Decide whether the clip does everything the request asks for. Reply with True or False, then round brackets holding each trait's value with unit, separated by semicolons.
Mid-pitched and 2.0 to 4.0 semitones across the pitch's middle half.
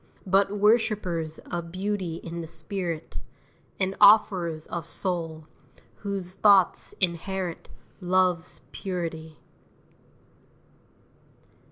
True (180 Hz; 2.9 semitones)